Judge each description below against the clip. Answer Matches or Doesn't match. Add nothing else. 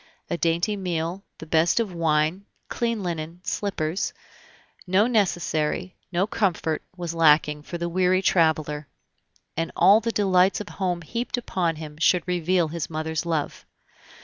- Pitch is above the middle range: Doesn't match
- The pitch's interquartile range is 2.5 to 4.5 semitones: Matches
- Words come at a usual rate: Matches